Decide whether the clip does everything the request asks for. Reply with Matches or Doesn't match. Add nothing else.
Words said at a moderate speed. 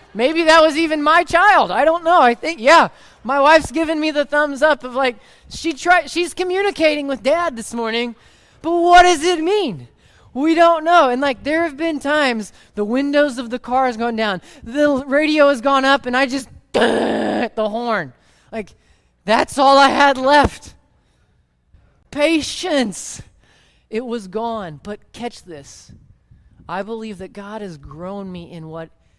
Matches